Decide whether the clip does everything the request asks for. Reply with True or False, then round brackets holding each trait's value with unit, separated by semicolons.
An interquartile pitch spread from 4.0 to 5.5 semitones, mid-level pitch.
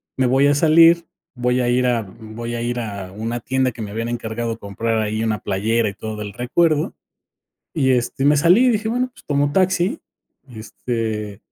False (4.6 semitones; 120 Hz)